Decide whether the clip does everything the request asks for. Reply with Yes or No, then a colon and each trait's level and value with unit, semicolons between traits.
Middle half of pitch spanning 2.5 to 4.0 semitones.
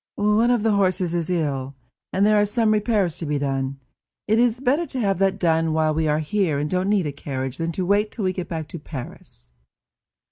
No: wide, 5.6 semitones